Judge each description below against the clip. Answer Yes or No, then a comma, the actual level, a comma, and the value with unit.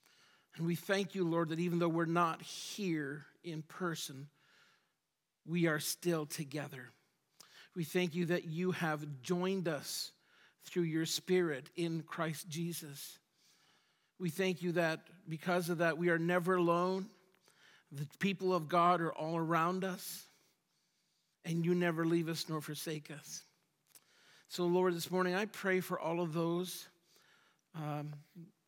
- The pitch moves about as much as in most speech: No, narrow, 2.0 semitones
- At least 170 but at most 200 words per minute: No, average, 145 wpm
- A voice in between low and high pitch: Yes, medium, 170 Hz